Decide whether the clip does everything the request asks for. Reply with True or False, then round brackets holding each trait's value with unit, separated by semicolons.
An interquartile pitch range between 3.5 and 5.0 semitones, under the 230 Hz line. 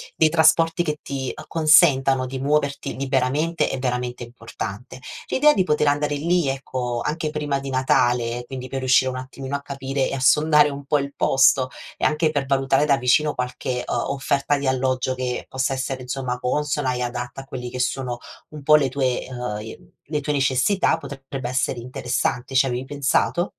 False (2.5 semitones; 135 Hz)